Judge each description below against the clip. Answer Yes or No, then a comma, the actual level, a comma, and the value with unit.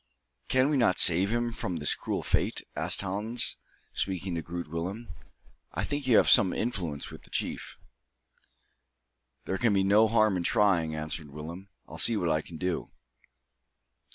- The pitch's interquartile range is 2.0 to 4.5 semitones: No, average, 5.0 semitones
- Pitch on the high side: No, very low, 95 Hz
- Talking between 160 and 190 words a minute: Yes, average, 165 wpm